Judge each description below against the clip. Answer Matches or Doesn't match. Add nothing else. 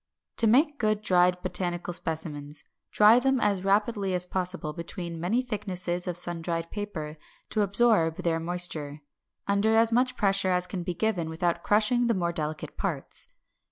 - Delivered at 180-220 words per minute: Doesn't match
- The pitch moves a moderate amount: Matches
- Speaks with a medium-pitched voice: Matches